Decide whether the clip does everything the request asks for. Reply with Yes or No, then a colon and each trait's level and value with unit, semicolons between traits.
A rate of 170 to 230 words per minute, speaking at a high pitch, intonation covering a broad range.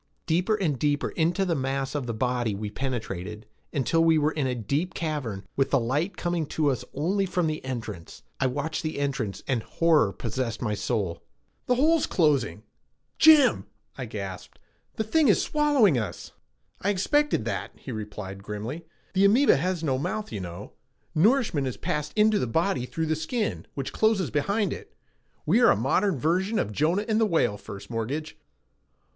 No: average, 175 wpm; medium, 150 Hz; wide, 7.8 semitones